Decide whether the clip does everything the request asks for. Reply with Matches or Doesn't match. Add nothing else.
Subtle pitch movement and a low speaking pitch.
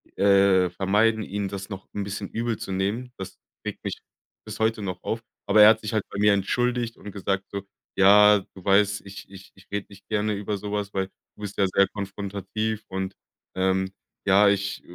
Matches